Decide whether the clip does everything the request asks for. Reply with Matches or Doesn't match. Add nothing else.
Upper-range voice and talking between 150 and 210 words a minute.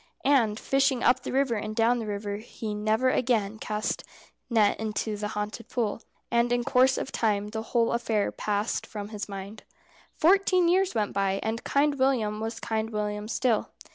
Matches